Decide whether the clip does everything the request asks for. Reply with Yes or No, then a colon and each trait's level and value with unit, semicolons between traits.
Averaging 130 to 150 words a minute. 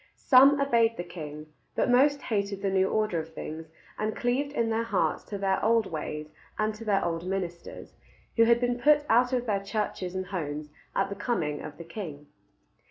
No: average, 195 wpm